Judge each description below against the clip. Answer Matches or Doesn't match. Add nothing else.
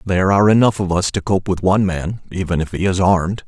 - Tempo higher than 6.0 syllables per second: Matches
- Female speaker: Doesn't match